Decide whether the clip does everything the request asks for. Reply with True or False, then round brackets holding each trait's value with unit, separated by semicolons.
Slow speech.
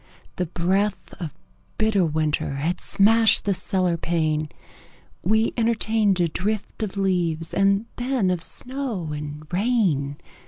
True (125 wpm)